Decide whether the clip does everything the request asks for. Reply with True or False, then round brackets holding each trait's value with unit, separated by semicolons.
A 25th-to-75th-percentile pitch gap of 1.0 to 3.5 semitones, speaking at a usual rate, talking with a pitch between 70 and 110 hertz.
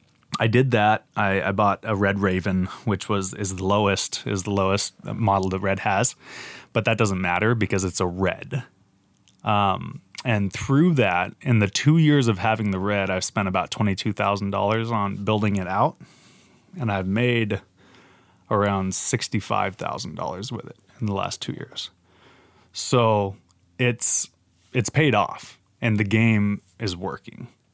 True (2.9 semitones; 165 wpm; 100 Hz)